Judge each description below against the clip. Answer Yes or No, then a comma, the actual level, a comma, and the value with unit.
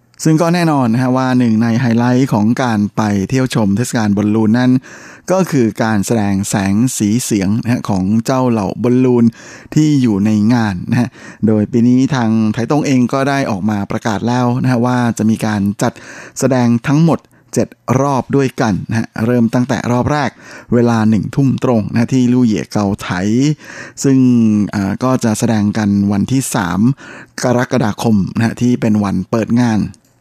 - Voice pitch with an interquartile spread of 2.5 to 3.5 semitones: Yes, average, 2.9 semitones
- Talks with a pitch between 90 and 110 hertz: No, low, 120 Hz